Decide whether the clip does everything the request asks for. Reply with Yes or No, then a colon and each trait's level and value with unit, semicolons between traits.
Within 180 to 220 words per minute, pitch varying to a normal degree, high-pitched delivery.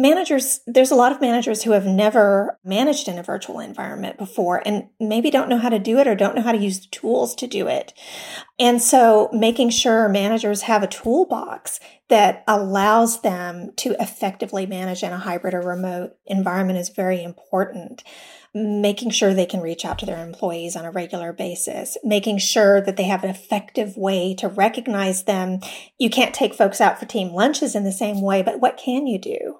Yes: average, 200 wpm; average, 3.7 semitones; high, 210 Hz